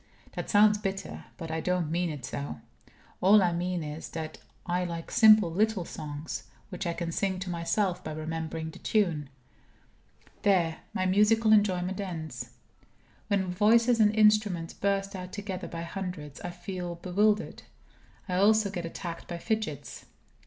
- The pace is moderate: Yes, average, 150 wpm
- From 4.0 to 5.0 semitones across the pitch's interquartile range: No, average, 3.5 semitones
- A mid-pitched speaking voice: Yes, medium, 180 Hz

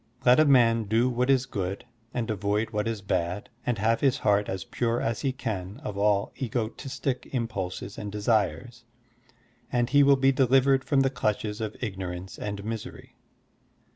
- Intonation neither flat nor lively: Yes, average, 3.8 semitones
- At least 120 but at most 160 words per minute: No, average, 170 wpm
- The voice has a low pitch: Yes, low, 115 Hz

